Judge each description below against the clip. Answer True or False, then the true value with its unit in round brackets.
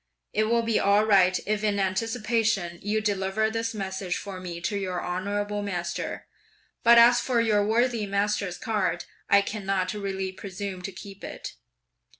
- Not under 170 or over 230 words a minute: False (155 wpm)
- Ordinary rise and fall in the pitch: False (2.3 semitones)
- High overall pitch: True (205 Hz)